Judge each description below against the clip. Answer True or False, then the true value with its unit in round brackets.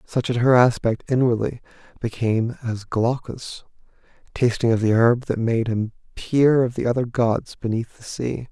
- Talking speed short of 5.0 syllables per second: True (4.6 syllables/s)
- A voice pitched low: True (120 Hz)